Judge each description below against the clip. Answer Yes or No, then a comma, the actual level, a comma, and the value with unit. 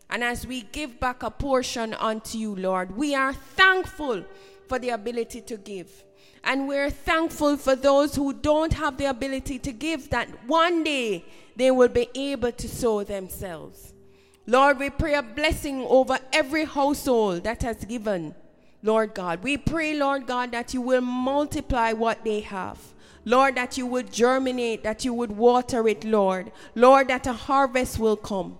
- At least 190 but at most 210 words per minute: No, average, 170 wpm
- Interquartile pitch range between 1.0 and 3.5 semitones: No, average, 4.0 semitones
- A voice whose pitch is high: Yes, very high, 250 Hz